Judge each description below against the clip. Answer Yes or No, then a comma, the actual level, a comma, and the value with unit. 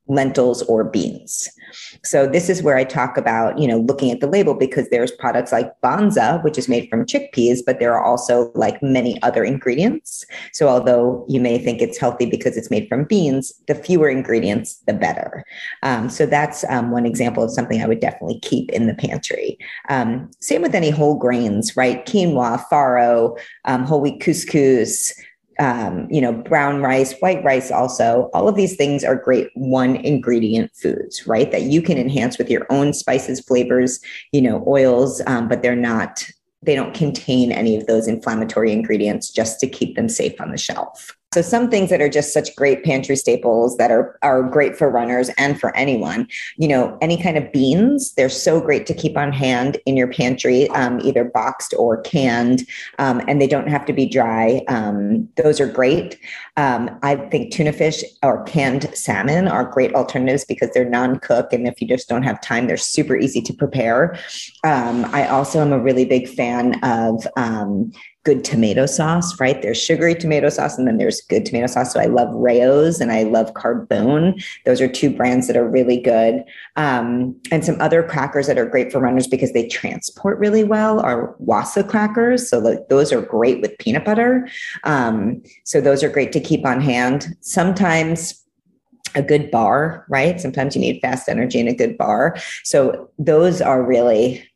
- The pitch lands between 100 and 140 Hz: Yes, low, 135 Hz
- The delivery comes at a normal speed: Yes, average, 190 wpm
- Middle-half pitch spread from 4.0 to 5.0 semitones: Yes, average, 4.4 semitones